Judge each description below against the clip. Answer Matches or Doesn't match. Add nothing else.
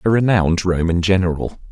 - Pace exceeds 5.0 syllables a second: Matches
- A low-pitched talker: Matches